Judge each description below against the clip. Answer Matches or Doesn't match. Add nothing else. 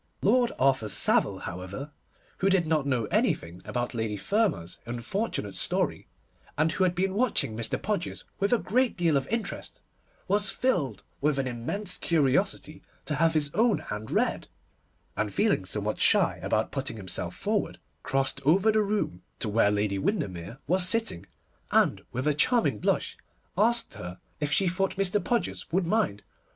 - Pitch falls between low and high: Matches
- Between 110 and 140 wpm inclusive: Doesn't match